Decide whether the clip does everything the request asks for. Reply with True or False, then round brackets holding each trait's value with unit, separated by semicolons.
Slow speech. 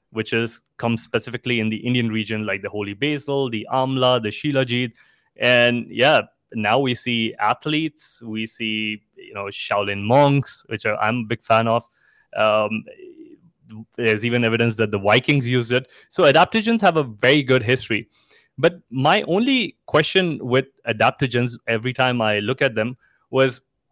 False (160 wpm)